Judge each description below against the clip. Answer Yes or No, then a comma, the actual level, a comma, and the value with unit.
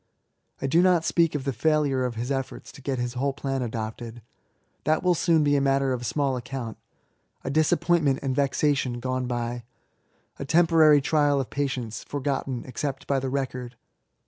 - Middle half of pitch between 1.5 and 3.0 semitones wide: Yes, average, 2.7 semitones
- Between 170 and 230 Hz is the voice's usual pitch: No, low, 135 Hz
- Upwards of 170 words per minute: Yes, average, 180 wpm